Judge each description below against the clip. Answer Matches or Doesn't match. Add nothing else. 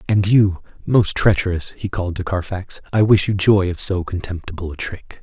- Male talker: Matches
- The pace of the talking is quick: Doesn't match